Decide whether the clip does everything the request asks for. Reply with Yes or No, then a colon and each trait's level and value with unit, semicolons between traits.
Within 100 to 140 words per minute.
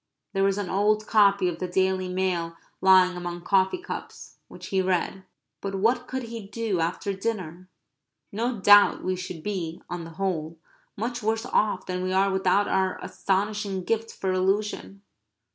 No: average, 165 wpm